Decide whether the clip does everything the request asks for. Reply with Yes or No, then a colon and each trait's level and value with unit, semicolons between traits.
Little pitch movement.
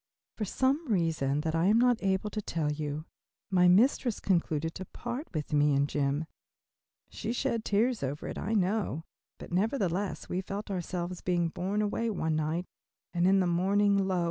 No: average, 4.6 semitones